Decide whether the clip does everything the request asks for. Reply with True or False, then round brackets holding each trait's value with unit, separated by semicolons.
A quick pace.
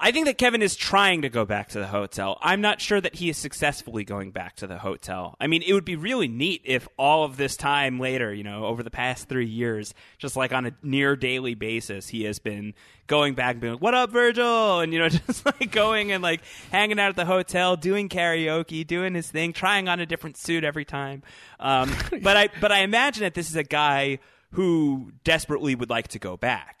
True (235 wpm)